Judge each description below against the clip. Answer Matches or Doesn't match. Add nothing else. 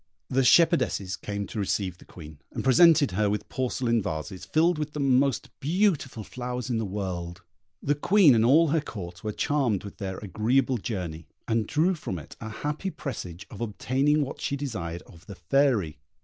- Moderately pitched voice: Doesn't match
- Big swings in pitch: Matches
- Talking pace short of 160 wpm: Doesn't match